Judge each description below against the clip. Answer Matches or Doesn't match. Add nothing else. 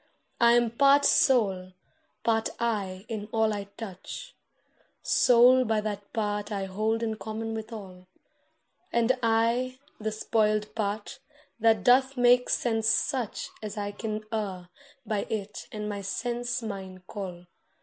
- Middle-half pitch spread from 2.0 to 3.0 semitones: Matches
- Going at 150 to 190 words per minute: Doesn't match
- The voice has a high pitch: Matches